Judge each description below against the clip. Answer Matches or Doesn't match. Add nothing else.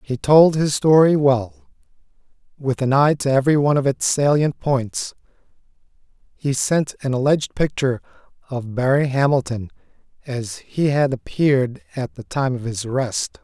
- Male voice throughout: Matches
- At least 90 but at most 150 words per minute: Matches